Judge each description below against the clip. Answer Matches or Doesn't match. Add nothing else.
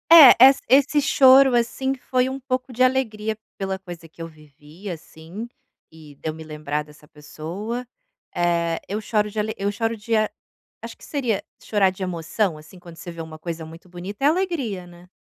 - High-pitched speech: Matches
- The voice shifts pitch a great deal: Matches